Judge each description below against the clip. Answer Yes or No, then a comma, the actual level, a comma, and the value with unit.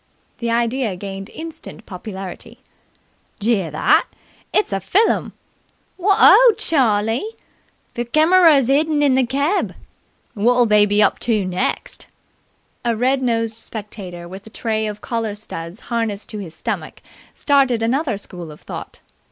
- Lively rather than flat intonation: No, average, 4.8 semitones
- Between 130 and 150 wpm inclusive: Yes, slow, 135 wpm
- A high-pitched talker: Yes, high, 225 Hz